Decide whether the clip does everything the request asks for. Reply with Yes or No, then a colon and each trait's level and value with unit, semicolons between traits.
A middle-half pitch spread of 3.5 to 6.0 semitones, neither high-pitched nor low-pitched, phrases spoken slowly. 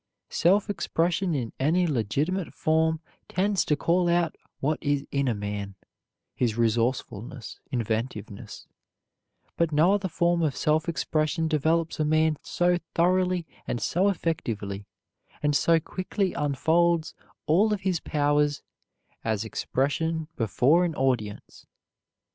Yes: average, 4.8 semitones; medium, 155 Hz; slow, 125 wpm